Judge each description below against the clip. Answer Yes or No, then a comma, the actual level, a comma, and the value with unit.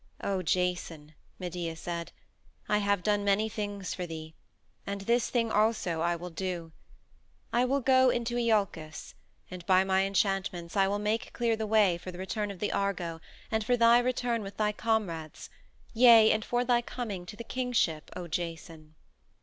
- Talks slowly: No, average, 175 wpm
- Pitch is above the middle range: Yes, high, 200 Hz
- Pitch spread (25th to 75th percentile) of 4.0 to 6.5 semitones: Yes, average, 4.3 semitones